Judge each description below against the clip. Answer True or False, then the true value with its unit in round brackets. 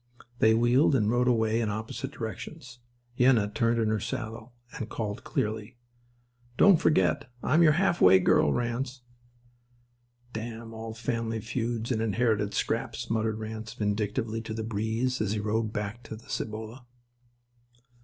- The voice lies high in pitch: False (115 Hz)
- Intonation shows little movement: True (1.9 semitones)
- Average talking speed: True (145 wpm)